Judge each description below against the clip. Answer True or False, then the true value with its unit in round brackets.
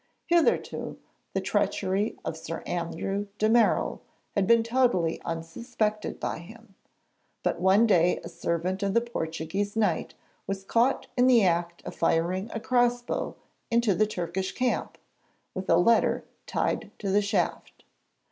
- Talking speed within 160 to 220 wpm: False (145 wpm)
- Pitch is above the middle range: True (200 Hz)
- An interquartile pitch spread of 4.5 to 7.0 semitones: True (4.8 semitones)